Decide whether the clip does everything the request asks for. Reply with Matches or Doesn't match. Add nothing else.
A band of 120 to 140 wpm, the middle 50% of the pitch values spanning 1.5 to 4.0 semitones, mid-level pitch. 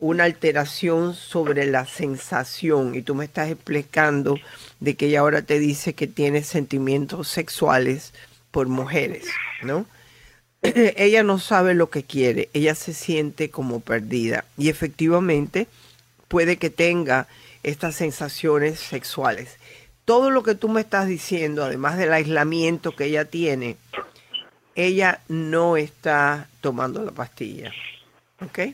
Matches